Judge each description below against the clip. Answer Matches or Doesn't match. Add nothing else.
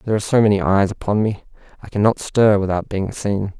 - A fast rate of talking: Matches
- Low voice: Matches